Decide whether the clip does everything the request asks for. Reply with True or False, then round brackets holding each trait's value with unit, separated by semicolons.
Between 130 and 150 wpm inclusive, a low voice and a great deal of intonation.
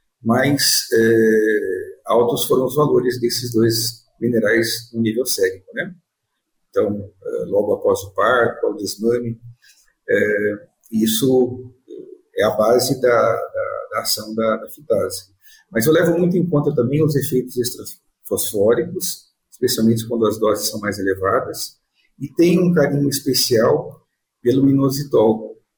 True (135 wpm; 130 Hz; 7.9 semitones)